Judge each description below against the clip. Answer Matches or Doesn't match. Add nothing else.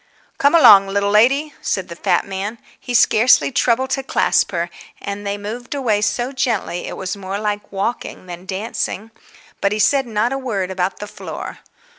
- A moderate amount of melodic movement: Matches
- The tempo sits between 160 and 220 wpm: Matches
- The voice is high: Matches